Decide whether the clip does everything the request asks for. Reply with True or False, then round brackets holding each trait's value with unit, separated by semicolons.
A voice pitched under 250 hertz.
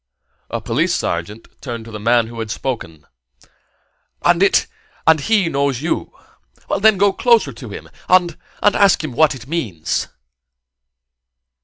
True (135 Hz)